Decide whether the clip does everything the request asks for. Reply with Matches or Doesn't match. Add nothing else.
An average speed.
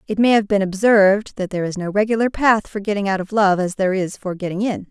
Doesn't match